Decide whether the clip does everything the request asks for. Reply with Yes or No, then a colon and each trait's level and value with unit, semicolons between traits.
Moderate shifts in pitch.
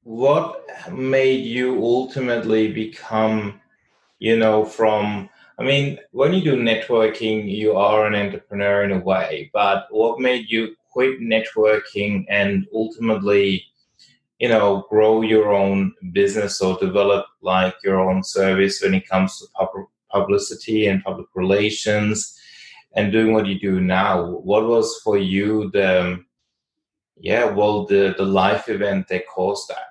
No: narrow, 2.3 semitones